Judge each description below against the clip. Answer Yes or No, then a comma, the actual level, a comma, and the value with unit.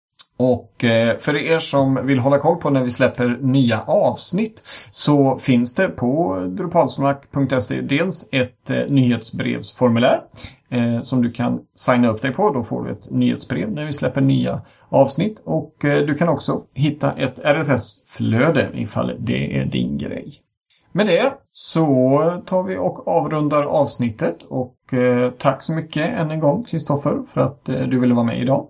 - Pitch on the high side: No, low, 135 Hz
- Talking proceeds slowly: No, average, 155 wpm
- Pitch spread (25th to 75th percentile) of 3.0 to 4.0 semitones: Yes, average, 3.7 semitones